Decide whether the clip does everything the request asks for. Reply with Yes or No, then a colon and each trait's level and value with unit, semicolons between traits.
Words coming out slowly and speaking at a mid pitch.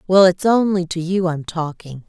No: average, 200 wpm; medium, 175 Hz